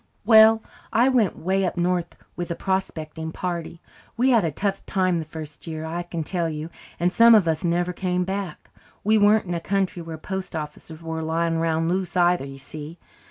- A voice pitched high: No, medium, 175 Hz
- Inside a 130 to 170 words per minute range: No, average, 200 wpm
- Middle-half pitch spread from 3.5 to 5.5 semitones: No, average, 2.9 semitones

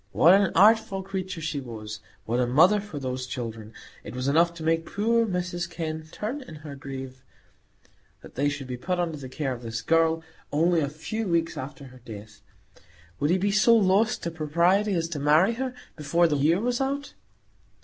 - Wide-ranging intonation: Yes, wide, 5.8 semitones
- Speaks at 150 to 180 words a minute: No, average, 195 wpm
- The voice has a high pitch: No, medium, 165 Hz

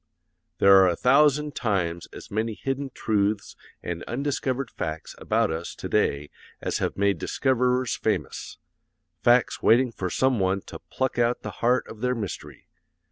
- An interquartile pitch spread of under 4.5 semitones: No, average, 5.0 semitones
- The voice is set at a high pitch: No, low, 115 Hz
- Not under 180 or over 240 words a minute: No, average, 155 wpm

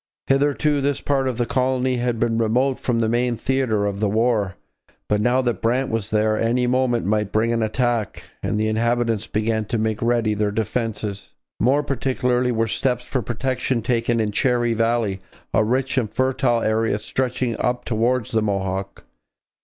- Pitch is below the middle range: Yes, low, 115 Hz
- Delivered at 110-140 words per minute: No, average, 175 wpm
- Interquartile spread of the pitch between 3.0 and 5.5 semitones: No, narrow, 2.6 semitones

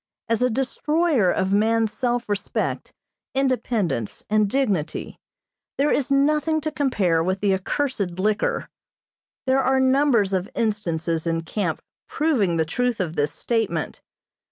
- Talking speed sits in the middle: No, slow, 130 wpm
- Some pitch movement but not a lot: No, wide, 6.2 semitones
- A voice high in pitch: Yes, high, 220 Hz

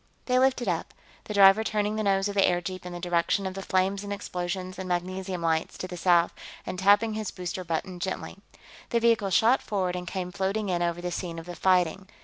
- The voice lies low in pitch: No, medium, 185 Hz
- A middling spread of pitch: No, narrow, 2.3 semitones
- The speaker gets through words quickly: Yes, fast, 220 wpm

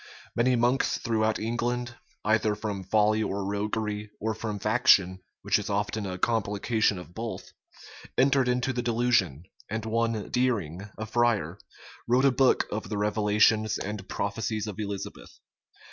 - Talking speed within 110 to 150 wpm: Yes, average, 145 wpm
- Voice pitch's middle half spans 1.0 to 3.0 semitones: Yes, narrow, 2.5 semitones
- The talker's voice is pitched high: No, low, 110 Hz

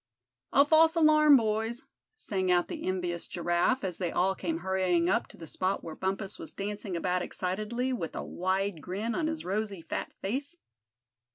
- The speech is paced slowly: No, average, 175 wpm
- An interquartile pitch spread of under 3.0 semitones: No, average, 4.8 semitones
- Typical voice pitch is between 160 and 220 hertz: Yes, high, 190 Hz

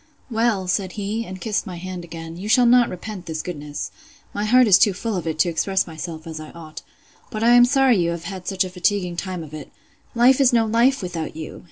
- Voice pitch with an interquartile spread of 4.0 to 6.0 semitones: Yes, average, 4.9 semitones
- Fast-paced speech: Yes, fast, 230 wpm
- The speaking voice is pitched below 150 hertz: No, medium, 185 Hz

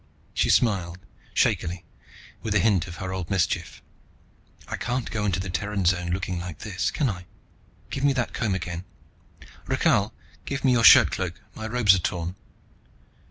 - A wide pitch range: No, average, 3.8 semitones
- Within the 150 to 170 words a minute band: Yes, average, 160 wpm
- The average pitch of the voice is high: No, very low, 95 Hz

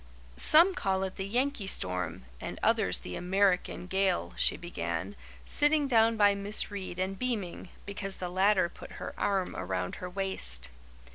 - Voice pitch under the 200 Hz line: Yes, high, 190 Hz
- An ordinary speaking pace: Yes, average, 155 wpm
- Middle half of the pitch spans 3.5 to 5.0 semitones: No, average, 2.7 semitones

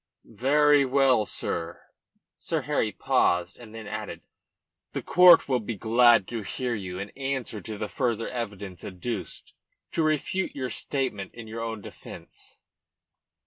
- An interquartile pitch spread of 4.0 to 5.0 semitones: Yes, average, 4.4 semitones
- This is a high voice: No, low, 115 Hz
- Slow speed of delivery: No, average, 145 wpm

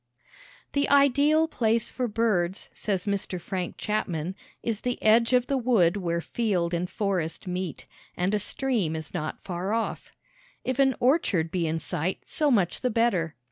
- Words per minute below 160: No, average, 165 wpm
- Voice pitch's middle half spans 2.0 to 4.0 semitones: No, wide, 5.6 semitones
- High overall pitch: Yes, high, 205 Hz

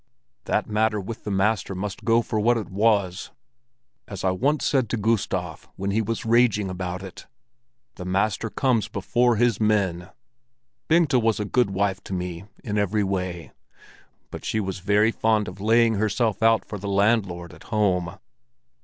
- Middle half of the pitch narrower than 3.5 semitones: Yes, average, 3.0 semitones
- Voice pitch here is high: No, low, 105 Hz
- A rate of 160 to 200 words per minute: Yes, average, 170 wpm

